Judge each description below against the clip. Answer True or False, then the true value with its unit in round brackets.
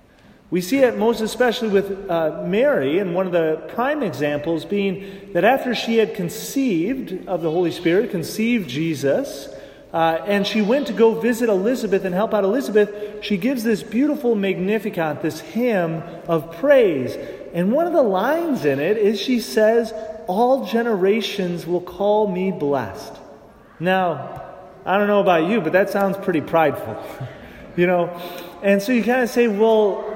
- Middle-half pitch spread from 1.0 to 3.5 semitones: False (4.4 semitones)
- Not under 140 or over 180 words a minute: True (165 wpm)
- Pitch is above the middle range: True (200 Hz)